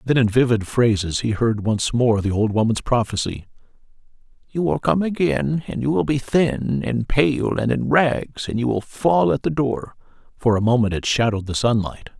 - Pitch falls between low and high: No, low, 115 Hz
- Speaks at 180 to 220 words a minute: Yes, average, 195 wpm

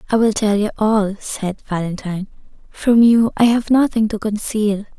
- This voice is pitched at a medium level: No, high, 215 Hz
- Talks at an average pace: Yes, average, 170 wpm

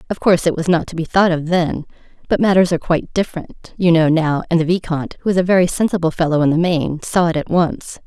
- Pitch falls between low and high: Yes, medium, 170 Hz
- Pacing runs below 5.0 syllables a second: No, 6.2 syllables/s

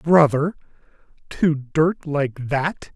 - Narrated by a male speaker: Yes, male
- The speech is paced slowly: Yes, slow, 80 wpm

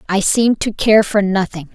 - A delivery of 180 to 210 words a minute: Yes, fast, 205 wpm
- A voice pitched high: Yes, high, 200 Hz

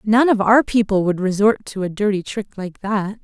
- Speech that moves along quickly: Yes, fast, 220 wpm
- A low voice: No, high, 205 Hz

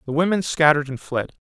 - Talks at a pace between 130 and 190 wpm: No, fast, 205 wpm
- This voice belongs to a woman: No, male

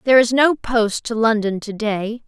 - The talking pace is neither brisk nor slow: No, fast, 210 wpm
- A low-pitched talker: No, high, 225 Hz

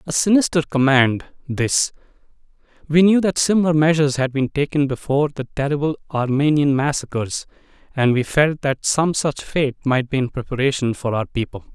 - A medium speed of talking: Yes, average, 160 wpm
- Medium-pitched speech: Yes, medium, 145 Hz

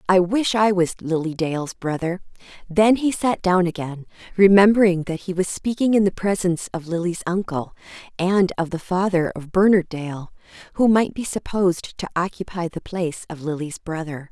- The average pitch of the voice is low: No, medium, 180 Hz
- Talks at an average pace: Yes, average, 170 wpm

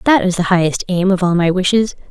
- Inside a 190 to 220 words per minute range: No, fast, 255 wpm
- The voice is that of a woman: Yes, female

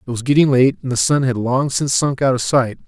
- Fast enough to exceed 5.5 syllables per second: Yes, 5.8 syllables/s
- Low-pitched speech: Yes, low, 130 Hz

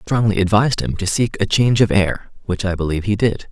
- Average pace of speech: No, fast, 255 wpm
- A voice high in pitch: No, low, 100 Hz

